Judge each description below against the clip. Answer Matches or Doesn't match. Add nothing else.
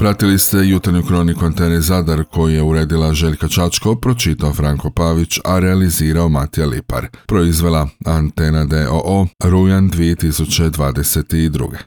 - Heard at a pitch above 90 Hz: Doesn't match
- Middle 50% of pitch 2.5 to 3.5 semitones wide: Matches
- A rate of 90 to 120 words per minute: Matches